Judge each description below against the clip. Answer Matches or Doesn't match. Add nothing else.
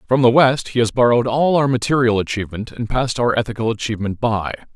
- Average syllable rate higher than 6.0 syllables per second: Matches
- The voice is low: Matches